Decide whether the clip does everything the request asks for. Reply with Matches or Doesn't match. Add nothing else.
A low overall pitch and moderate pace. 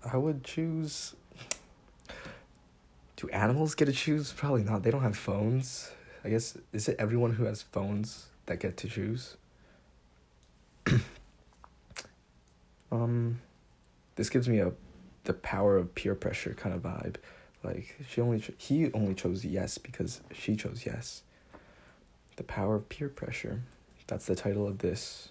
Matches